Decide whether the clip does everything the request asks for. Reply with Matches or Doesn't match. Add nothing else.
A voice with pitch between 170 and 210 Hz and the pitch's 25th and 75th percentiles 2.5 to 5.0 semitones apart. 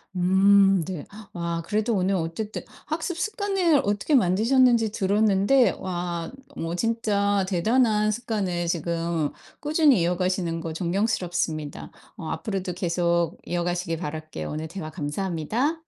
Matches